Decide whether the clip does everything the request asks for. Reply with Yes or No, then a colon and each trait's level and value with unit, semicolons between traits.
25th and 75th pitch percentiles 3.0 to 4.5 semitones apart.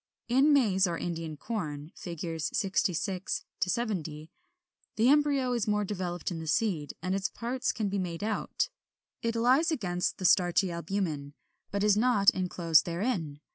No: average, 5.1 semitones